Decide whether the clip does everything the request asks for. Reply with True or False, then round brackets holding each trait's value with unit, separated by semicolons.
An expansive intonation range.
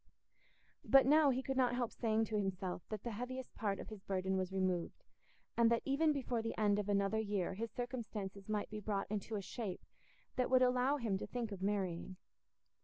False (4.0 semitones)